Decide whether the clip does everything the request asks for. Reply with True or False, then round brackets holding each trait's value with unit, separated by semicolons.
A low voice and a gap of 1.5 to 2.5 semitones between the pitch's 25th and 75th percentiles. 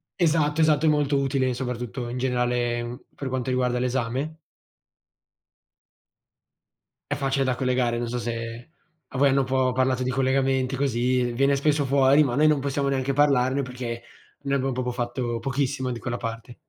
True (130 Hz; 2.0 semitones)